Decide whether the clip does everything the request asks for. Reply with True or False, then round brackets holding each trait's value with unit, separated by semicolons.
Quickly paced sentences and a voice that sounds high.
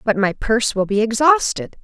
False (195 wpm; 225 Hz)